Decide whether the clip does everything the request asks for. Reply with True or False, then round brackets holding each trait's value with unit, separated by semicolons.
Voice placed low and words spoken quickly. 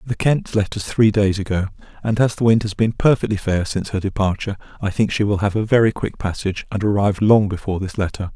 True (105 Hz; 235 wpm)